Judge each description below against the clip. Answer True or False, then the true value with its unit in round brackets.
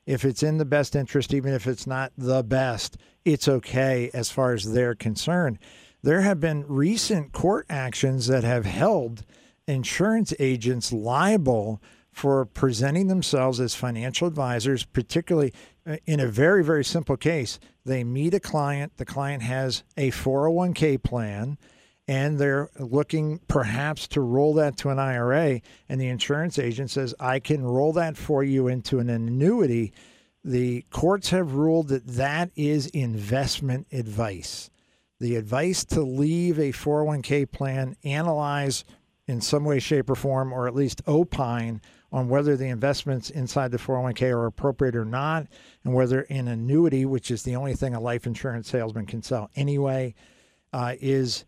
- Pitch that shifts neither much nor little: True (3.0 semitones)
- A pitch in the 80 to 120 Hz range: False (135 Hz)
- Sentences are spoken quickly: False (155 wpm)